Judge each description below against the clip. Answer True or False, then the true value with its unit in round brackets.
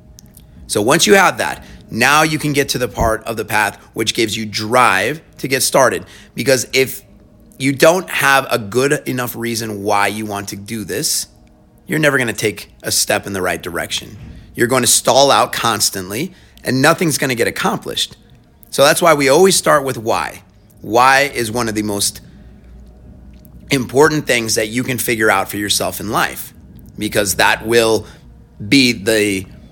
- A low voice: True (115 Hz)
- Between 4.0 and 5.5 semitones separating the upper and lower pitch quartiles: True (4.7 semitones)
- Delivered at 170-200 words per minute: True (180 wpm)